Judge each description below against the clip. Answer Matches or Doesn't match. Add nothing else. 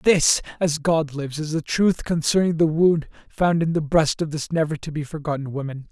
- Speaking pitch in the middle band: Matches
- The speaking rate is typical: Doesn't match